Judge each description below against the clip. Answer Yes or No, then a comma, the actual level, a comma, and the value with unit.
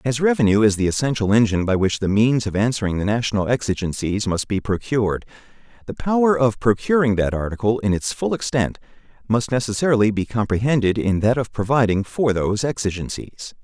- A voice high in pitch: No, low, 110 Hz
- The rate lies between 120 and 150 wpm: No, average, 170 wpm